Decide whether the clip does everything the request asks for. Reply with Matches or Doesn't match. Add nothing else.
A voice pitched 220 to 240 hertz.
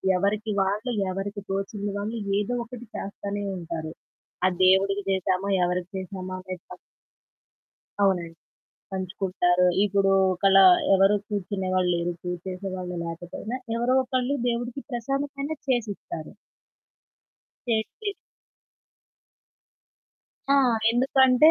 Doesn't match